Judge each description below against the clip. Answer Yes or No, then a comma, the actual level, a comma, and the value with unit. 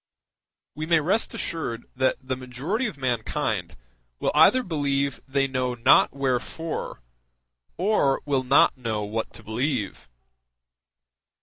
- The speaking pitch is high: No, low, 135 Hz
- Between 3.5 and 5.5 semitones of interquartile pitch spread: Yes, average, 3.9 semitones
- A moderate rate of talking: No, slow, 120 wpm